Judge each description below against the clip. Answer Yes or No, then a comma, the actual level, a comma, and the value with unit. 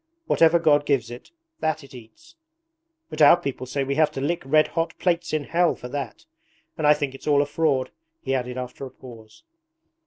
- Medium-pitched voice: Yes, medium, 145 Hz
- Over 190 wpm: Yes, fast, 205 wpm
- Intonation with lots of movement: No, average, 3.3 semitones